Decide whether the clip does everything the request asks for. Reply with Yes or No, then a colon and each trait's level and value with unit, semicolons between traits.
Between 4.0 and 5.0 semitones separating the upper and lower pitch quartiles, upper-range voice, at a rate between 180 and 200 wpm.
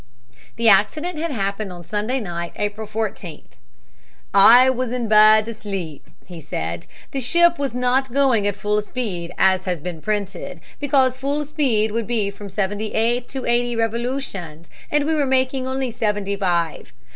No: average, 4.7 semitones; high, 220 Hz; average, 165 wpm